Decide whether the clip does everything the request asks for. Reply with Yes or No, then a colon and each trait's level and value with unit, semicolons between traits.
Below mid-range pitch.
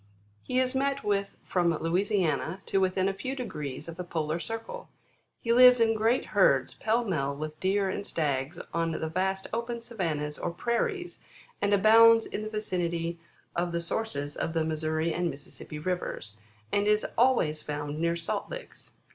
No: medium, 185 Hz